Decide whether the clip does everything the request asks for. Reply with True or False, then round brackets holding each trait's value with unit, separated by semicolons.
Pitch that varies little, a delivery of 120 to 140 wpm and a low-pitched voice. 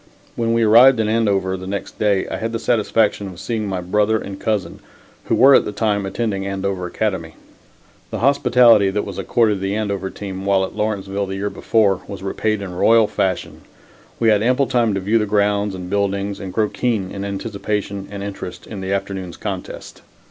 False (2.1 semitones; 195 wpm; 100 Hz)